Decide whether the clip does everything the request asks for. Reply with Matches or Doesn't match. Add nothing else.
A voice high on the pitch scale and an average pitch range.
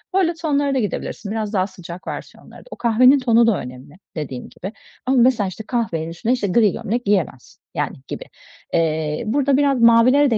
Doesn't match